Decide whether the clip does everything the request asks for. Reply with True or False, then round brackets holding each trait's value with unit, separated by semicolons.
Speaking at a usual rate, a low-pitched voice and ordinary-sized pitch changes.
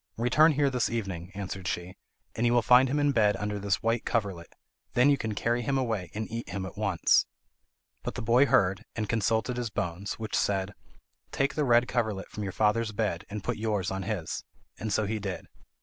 False (210 wpm; 110 Hz; 3.4 semitones)